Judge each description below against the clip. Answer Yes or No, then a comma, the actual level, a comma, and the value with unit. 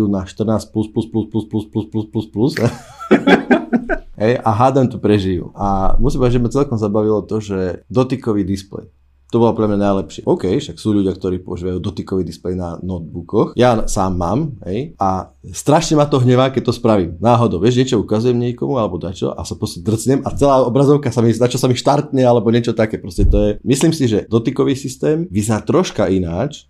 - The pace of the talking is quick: Yes, fast, 200 wpm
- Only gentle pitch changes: No, average, 4.2 semitones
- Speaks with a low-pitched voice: Yes, low, 110 Hz